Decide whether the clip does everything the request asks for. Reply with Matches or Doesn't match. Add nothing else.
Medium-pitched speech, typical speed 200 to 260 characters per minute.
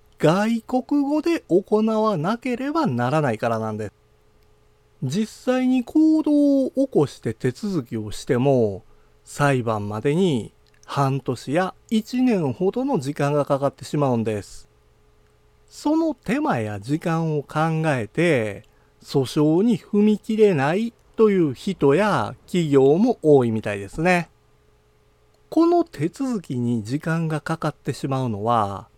Matches